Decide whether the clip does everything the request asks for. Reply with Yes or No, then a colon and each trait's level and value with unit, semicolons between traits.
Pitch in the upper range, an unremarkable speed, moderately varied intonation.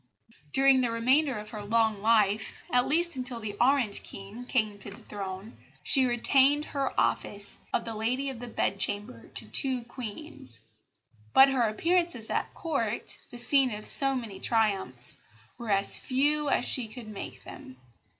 Yes: high, 235 Hz; average, 160 wpm; average, 4.2 semitones